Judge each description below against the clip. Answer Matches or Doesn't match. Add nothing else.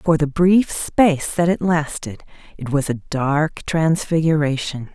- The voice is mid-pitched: Matches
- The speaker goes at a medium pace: Matches